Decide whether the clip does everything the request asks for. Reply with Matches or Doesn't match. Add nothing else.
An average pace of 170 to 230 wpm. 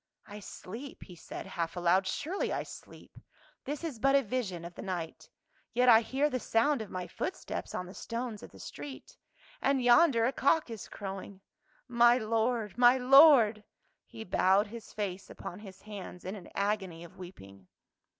Matches